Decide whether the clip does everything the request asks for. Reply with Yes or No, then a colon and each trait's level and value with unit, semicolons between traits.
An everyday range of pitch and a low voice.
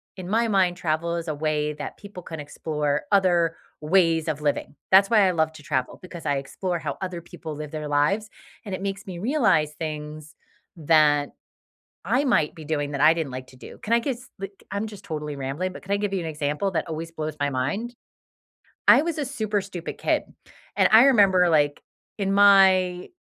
No: average, 4.6 semitones; medium, 170 Hz